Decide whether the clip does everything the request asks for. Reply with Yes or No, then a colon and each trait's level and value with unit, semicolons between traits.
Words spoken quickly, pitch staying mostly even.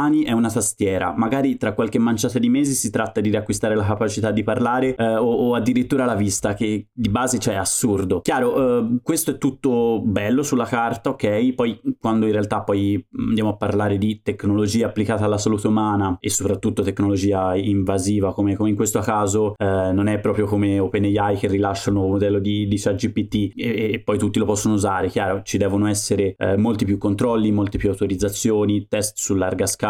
Yes: fast, 195 wpm; narrow, 2.3 semitones